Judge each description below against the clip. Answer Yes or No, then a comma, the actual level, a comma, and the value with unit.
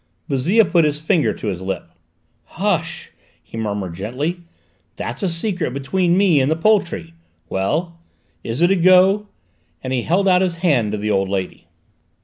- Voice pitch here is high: No, medium, 160 Hz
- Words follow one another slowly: No, average, 165 wpm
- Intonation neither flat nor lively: No, wide, 8.3 semitones